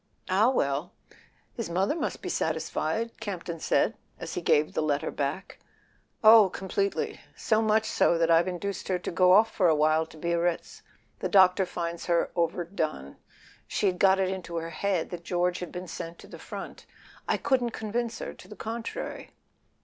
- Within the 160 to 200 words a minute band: Yes, average, 175 wpm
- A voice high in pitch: No, medium, 180 Hz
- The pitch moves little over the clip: No, average, 3.5 semitones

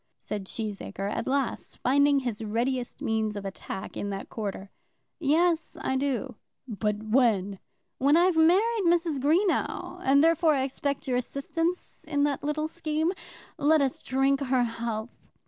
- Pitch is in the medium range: No, very high, 270 Hz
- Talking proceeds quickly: No, average, 145 wpm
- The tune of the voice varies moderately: No, wide, 5.9 semitones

